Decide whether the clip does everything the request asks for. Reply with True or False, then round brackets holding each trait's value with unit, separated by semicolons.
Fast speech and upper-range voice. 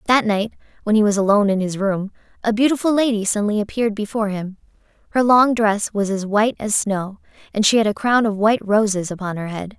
True (215 wpm; 210 Hz)